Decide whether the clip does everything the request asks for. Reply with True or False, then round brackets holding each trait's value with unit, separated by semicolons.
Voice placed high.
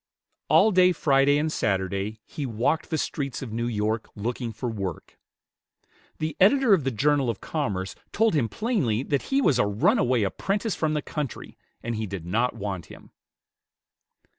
False (125 Hz)